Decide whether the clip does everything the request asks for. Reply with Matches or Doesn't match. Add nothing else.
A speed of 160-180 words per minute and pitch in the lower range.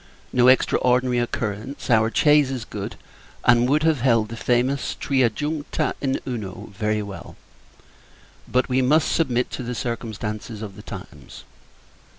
Doesn't match